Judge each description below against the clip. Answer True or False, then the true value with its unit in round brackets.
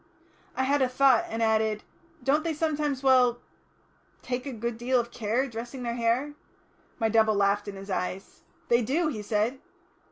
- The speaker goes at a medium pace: True (170 wpm)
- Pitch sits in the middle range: False (240 Hz)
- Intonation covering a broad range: False (3.5 semitones)